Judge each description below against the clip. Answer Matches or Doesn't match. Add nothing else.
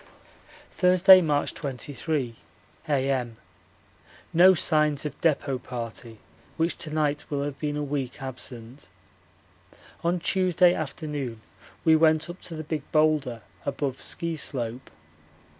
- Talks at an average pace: Doesn't match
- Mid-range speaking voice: Matches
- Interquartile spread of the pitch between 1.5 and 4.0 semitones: Matches